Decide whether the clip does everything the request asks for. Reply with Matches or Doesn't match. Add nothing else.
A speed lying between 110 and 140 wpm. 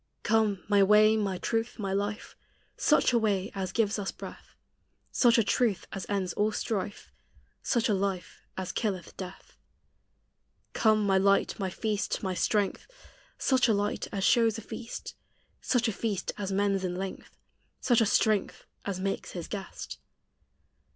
Doesn't match